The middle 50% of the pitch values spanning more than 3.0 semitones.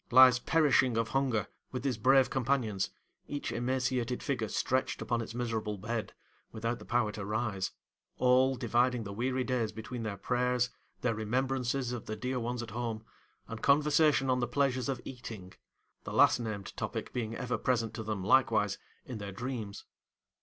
No: average, 2.7 semitones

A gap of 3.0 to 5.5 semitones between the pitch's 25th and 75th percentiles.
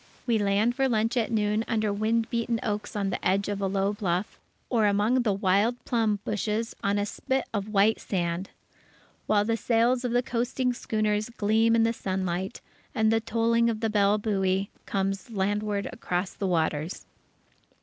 No: narrow, 2.5 semitones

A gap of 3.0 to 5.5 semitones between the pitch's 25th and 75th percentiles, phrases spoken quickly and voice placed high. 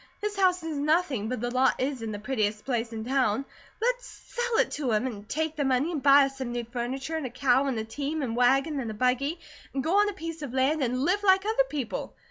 Yes: average, 4.7 semitones; fast, 255 wpm; very high, 270 Hz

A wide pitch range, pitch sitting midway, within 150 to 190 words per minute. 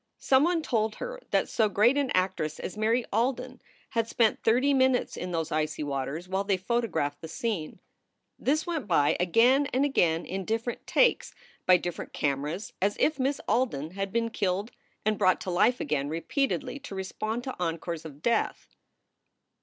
No: wide, 6.6 semitones; high, 215 Hz; average, 170 wpm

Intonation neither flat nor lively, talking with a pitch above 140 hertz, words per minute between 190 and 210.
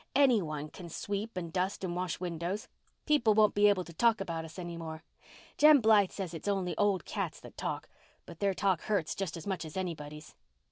Yes: average, 3.5 semitones; medium, 185 Hz; fast, 205 wpm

